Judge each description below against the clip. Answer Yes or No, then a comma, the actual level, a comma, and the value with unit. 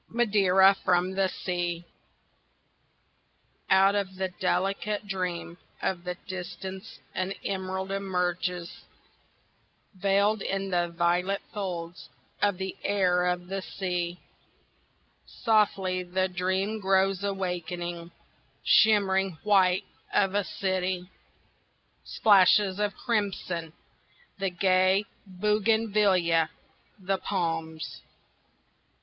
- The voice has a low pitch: No, high, 190 Hz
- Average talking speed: No, slow, 90 wpm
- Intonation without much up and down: Yes, narrow, 1.7 semitones